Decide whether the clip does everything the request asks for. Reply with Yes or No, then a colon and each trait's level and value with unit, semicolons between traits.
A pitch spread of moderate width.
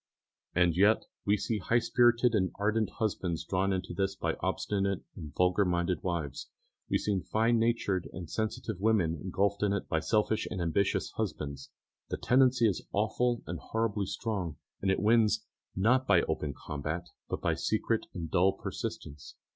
Yes: average, 3.9 semitones